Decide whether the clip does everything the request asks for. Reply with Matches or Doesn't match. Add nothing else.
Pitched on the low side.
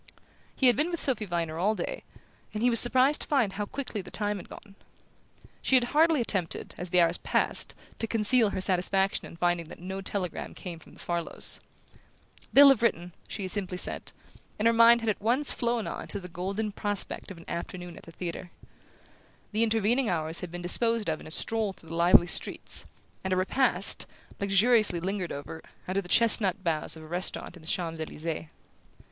Doesn't match